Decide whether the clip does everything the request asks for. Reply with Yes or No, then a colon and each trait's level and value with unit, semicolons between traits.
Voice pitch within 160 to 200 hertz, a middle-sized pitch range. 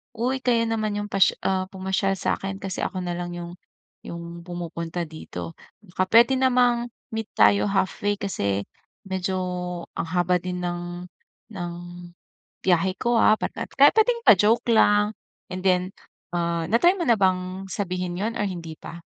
Yes: high, 190 Hz; average, 3.6 semitones